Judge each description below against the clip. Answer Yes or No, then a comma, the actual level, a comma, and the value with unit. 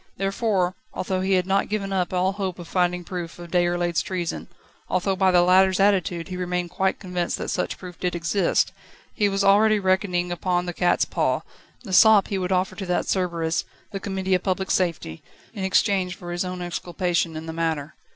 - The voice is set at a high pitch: No, medium, 180 Hz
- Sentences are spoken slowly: No, average, 195 wpm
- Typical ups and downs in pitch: No, narrow, 1.5 semitones